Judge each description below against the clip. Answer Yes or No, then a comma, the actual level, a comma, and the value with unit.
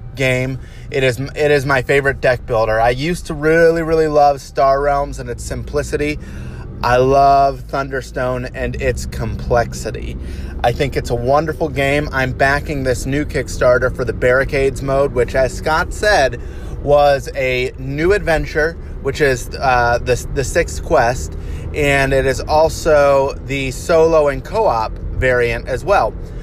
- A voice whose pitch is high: No, low, 135 Hz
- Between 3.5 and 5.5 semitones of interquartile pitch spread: No, narrow, 2.6 semitones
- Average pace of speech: Yes, average, 150 wpm